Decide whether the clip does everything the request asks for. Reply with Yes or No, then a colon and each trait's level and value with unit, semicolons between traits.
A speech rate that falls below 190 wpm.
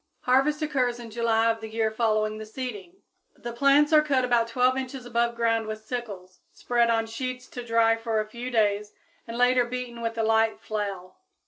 No: average, 195 wpm